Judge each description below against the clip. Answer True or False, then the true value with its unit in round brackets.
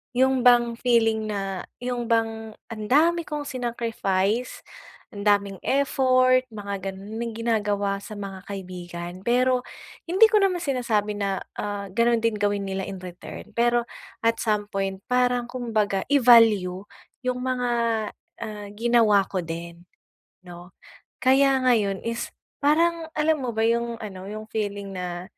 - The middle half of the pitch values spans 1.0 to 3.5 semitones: False (3.9 semitones)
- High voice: True (220 Hz)